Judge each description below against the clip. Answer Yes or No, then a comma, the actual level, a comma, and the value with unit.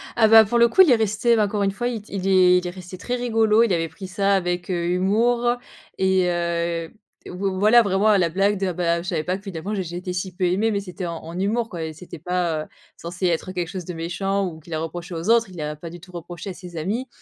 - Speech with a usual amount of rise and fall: Yes, average, 3.2 semitones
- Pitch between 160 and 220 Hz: Yes, medium, 185 Hz